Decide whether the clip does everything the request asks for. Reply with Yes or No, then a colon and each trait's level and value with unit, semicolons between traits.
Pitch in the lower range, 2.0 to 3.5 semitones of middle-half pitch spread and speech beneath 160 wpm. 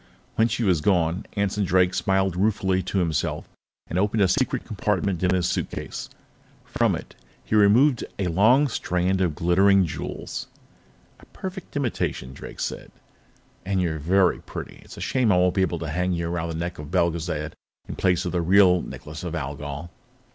No: very low, 90 Hz; average, 2.7 semitones; average, 175 wpm